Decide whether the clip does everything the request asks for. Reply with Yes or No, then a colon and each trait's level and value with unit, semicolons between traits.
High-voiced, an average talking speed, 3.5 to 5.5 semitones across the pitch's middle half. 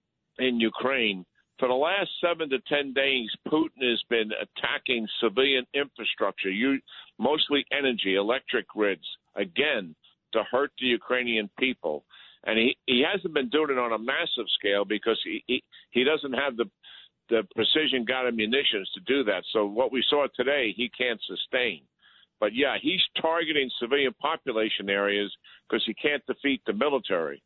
No: low, 130 Hz; average, 155 wpm; average, 4.1 semitones